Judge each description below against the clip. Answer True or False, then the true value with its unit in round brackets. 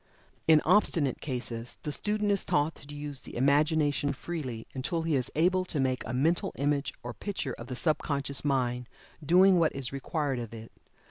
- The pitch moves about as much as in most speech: True (3.9 semitones)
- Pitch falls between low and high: True (145 Hz)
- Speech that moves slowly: False (185 wpm)